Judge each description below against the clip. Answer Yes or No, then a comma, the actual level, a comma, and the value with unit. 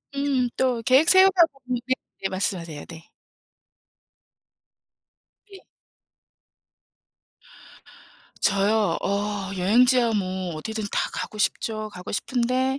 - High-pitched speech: Yes, high, 220 Hz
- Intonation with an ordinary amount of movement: Yes, average, 4.9 semitones